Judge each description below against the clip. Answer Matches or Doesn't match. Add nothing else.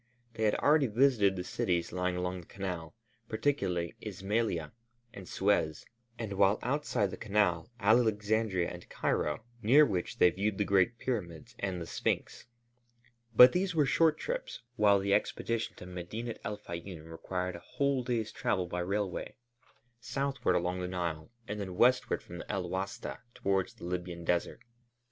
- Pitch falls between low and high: Doesn't match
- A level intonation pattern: Doesn't match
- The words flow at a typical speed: Matches